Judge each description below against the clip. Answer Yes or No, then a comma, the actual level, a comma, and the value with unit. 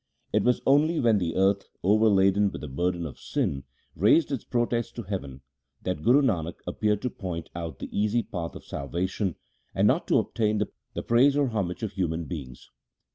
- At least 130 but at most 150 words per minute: No, average, 185 wpm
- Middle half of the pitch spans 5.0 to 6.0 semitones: Yes, average, 5.3 semitones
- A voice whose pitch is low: Yes, low, 100 Hz